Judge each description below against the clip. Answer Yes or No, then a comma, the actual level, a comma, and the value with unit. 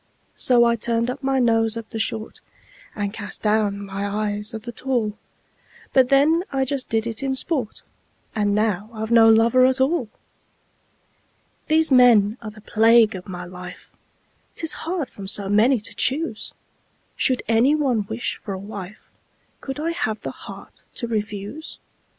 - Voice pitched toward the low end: No, high, 225 Hz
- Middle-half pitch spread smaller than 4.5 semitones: Yes, average, 3.9 semitones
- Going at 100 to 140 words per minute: No, average, 165 wpm